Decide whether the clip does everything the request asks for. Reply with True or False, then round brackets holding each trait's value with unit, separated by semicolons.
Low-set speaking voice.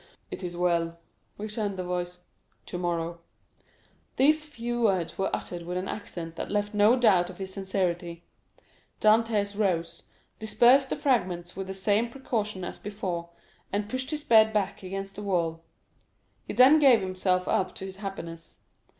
False (195 Hz)